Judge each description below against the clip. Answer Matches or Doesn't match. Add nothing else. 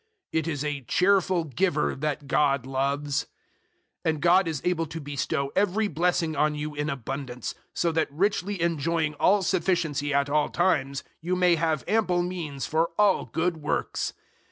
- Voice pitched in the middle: Matches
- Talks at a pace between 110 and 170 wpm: Matches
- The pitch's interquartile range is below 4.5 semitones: Matches